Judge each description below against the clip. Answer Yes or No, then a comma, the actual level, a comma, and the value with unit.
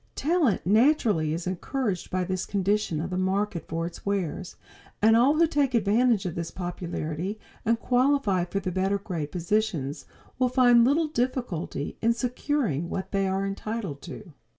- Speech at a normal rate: Yes, average, 160 wpm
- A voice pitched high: Yes, high, 200 Hz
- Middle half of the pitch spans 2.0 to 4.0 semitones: No, wide, 5.4 semitones